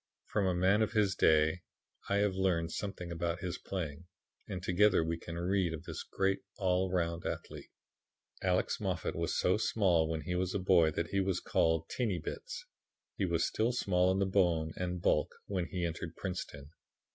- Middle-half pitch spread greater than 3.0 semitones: No, narrow, 2.4 semitones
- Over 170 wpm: Yes, average, 180 wpm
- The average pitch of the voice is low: Yes, very low, 90 Hz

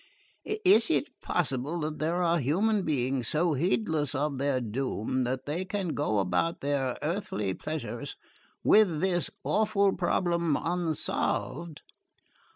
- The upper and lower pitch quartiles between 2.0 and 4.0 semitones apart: No, average, 4.7 semitones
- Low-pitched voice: No, medium, 155 Hz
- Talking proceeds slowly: Yes, slow, 125 wpm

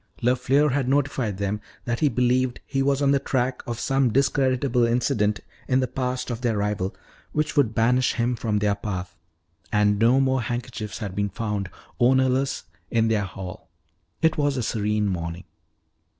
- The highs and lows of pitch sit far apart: No, average, 3.9 semitones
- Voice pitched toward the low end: Yes, low, 120 Hz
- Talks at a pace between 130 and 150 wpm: No, average, 165 wpm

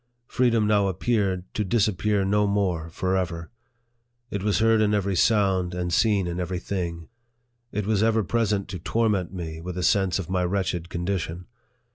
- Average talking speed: Yes, average, 165 wpm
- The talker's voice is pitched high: No, very low, 95 Hz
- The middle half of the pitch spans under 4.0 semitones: Yes, average, 2.9 semitones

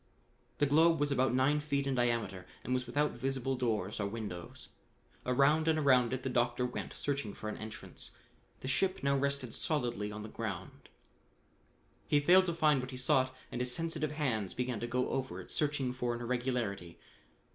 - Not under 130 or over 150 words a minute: No, average, 185 wpm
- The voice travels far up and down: No, average, 3.3 semitones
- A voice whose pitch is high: No, low, 130 Hz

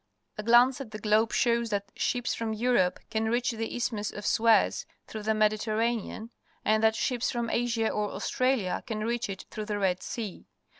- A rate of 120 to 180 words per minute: No, average, 190 wpm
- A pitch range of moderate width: No, narrow, 1.9 semitones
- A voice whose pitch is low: No, high, 220 Hz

